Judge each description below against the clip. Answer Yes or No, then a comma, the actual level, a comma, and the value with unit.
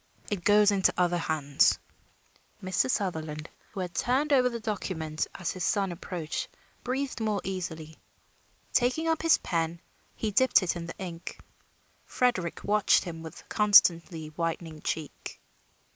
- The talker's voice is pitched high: No, medium, 180 Hz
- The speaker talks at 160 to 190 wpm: No, average, 140 wpm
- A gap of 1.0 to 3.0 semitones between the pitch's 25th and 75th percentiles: No, average, 4.4 semitones